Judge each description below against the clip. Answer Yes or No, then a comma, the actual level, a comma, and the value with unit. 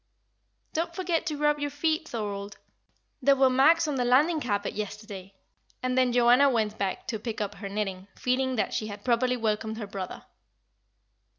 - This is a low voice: No, high, 245 Hz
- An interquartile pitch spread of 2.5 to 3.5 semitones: No, average, 5.2 semitones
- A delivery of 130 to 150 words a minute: No, average, 175 wpm